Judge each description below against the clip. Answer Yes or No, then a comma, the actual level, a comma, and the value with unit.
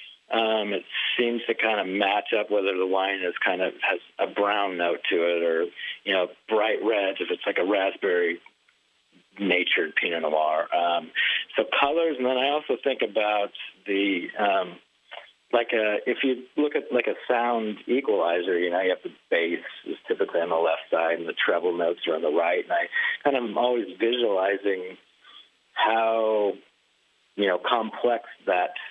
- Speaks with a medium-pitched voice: No, low, 120 Hz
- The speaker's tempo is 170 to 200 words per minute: Yes, average, 180 wpm